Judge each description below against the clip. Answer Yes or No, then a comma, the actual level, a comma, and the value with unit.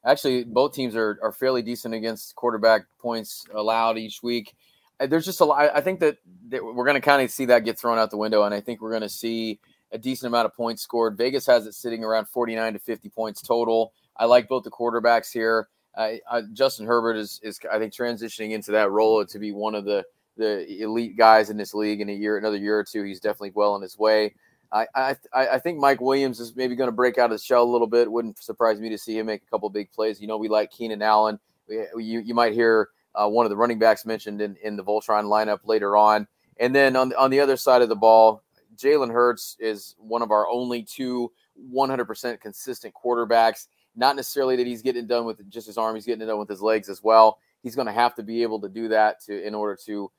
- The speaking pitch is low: Yes, low, 115 Hz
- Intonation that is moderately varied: No, narrow, 2.1 semitones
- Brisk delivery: Yes, fast, 250 wpm